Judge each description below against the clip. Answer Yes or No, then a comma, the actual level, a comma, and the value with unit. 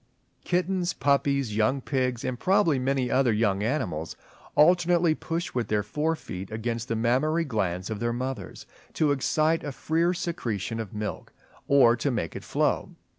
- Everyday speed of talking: Yes, average, 155 wpm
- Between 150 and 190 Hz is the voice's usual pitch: No, low, 130 Hz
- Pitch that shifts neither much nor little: No, wide, 5.9 semitones